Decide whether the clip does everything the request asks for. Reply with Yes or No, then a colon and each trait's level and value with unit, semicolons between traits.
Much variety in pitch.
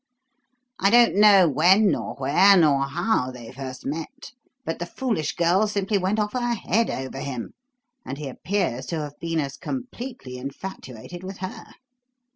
Yes: wide, 7.0 semitones